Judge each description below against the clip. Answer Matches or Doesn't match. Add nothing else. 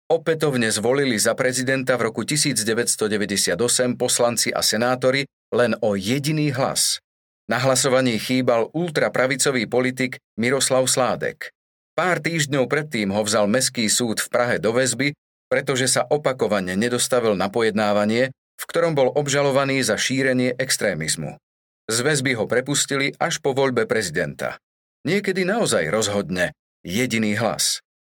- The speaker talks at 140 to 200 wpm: Doesn't match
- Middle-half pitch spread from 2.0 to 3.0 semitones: Doesn't match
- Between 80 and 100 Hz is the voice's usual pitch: Doesn't match